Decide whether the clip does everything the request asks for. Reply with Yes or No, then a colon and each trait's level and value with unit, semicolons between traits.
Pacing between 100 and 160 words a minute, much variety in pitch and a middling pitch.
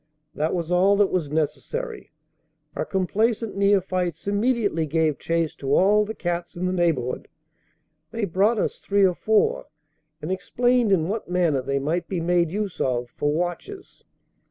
No: average, 155 wpm; average, 4.0 semitones; medium, 180 Hz